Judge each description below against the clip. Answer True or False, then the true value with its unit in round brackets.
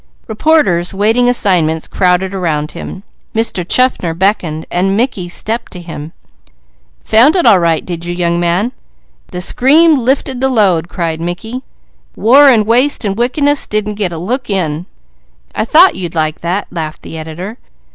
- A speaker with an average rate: True (155 wpm)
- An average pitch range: False (6.0 semitones)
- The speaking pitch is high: True (195 Hz)